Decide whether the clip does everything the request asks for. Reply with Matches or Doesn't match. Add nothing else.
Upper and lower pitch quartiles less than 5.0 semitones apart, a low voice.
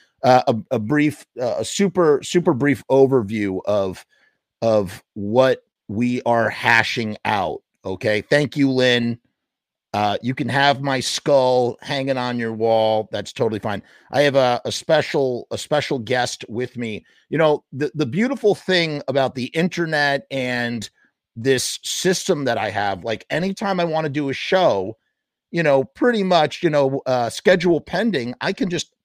Matches